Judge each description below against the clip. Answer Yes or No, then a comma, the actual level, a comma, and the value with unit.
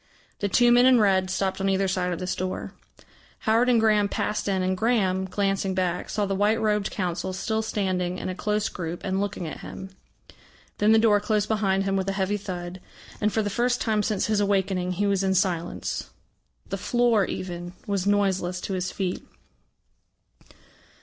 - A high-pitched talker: Yes, high, 195 Hz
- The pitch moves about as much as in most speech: No, narrow, 2.1 semitones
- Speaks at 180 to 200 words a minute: Yes, average, 190 wpm